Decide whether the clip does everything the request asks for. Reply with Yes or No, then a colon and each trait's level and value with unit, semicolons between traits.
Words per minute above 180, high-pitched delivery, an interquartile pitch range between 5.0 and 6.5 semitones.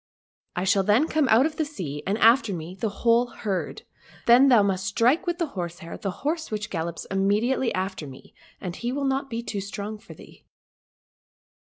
Yes: average, 190 wpm; high, 210 Hz; average, 5.3 semitones